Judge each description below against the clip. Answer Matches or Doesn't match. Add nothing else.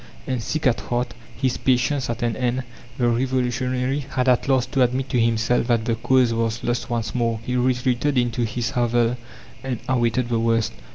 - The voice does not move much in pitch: Matches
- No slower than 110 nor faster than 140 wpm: Doesn't match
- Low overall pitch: Matches